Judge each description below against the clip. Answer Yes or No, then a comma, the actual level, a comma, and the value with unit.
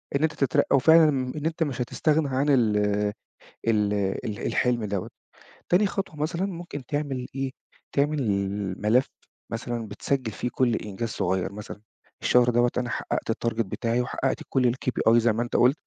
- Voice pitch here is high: No, low, 125 Hz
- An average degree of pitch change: Yes, average, 4.2 semitones